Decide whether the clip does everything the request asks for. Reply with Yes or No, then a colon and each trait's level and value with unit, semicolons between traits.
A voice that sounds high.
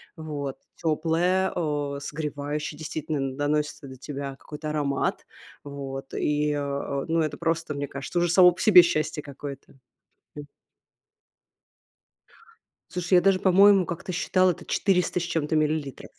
No: medium, 150 Hz